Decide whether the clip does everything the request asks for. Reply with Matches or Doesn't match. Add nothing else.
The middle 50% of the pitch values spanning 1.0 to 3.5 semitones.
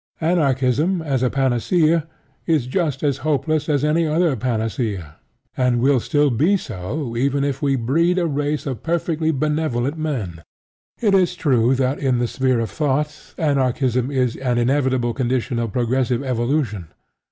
Doesn't match